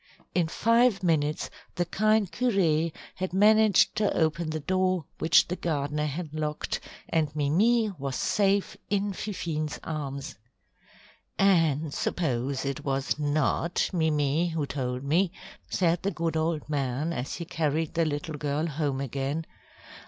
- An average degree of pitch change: Yes, average, 3.8 semitones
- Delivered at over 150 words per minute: No, slow, 135 wpm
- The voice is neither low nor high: Yes, medium, 160 Hz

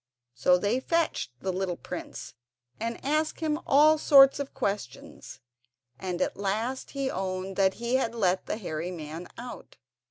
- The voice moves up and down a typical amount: No, wide, 6.7 semitones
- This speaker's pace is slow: No, average, 155 wpm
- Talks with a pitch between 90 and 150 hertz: No, high, 205 Hz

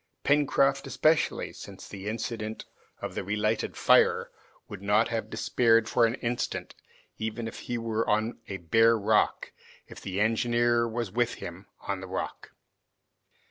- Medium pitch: No, low, 115 Hz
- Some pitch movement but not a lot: No, narrow, 2.1 semitones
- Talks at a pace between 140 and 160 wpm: Yes, average, 145 wpm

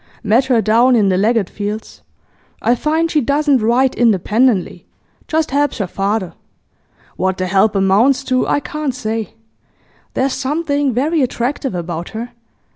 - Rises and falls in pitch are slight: No, average, 5.0 semitones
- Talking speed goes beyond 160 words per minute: No, average, 145 wpm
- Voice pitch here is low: No, high, 240 Hz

